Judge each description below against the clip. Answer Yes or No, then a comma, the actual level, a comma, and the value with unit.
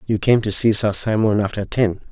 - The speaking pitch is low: Yes, low, 105 Hz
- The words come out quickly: Yes, fast, 225 wpm